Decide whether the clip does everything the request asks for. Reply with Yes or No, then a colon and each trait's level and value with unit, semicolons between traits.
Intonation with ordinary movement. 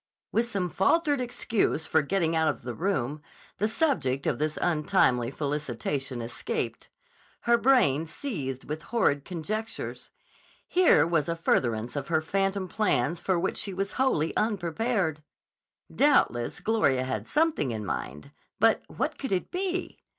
No: wide, 7.7 semitones